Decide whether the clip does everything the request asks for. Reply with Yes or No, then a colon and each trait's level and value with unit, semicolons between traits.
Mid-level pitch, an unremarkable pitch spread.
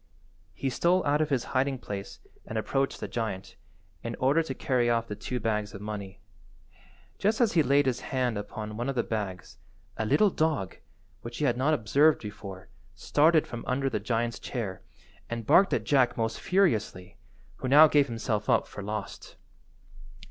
No: low, 120 Hz; average, 4.9 semitones